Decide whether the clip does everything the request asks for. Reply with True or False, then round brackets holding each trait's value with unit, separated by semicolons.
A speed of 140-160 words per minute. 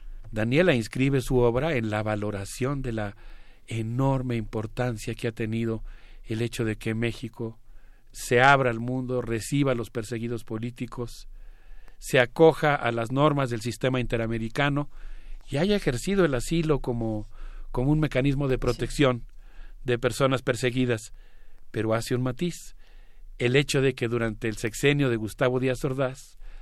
True (145 wpm)